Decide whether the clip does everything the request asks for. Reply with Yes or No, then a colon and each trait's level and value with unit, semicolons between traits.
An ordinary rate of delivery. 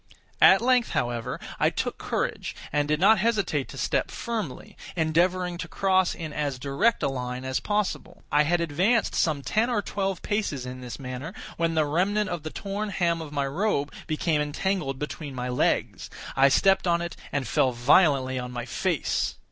Yes: average, 180 wpm